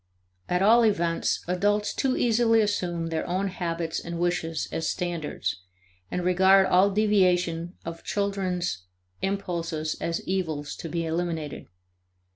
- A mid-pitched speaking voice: Yes, medium, 180 Hz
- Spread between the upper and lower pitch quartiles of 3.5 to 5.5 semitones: No, average, 2.9 semitones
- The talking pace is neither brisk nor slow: No, slow, 125 wpm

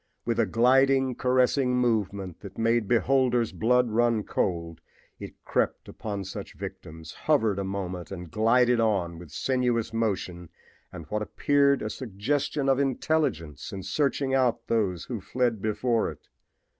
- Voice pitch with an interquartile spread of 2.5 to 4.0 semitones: No, average, 4.6 semitones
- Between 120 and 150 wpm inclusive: Yes, average, 145 wpm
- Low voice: Yes, low, 115 Hz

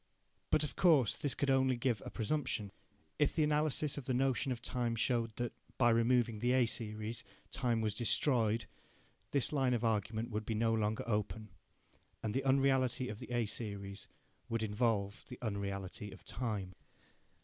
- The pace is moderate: Yes, average, 170 wpm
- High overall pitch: No, low, 115 Hz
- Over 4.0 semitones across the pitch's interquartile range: No, average, 3.3 semitones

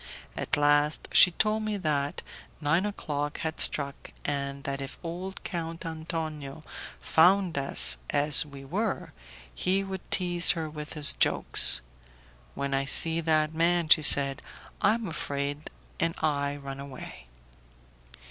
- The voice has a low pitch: No, medium, 155 Hz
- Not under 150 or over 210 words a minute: No, average, 140 wpm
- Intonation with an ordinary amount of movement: Yes, average, 3.2 semitones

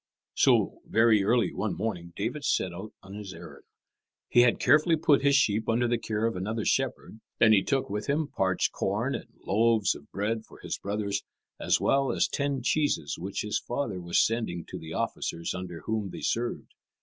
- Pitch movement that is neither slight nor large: Yes, average, 3.8 semitones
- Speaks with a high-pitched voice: No, low, 110 Hz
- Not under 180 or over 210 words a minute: Yes, average, 190 wpm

